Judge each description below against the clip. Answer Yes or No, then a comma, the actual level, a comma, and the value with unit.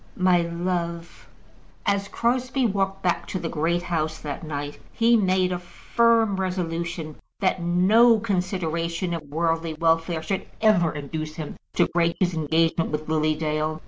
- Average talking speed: Yes, average, 145 wpm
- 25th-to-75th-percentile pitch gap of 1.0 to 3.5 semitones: Yes, average, 3.0 semitones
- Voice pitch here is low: No, medium, 170 Hz